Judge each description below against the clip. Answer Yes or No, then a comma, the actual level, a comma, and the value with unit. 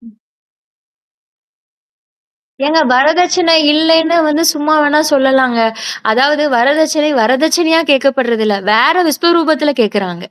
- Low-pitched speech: No, very high, 295 Hz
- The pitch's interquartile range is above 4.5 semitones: No, average, 4.2 semitones